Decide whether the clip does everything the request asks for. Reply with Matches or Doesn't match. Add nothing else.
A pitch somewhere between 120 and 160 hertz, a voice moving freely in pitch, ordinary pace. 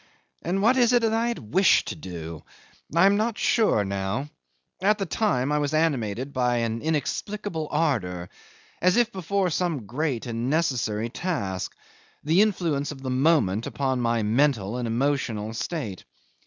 Matches